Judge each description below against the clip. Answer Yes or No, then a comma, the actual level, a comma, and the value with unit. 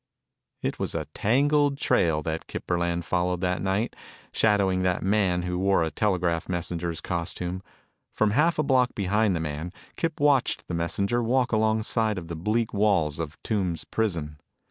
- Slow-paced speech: No, average, 165 wpm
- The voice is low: Yes, very low, 95 Hz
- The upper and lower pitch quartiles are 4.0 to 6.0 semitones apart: Yes, average, 4.4 semitones